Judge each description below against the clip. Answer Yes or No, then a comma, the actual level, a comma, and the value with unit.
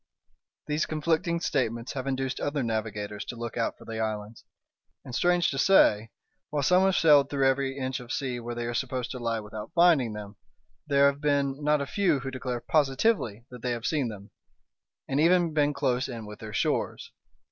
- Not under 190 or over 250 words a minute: Yes, average, 195 wpm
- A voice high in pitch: No, low, 135 Hz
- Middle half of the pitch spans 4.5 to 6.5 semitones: No, average, 4.1 semitones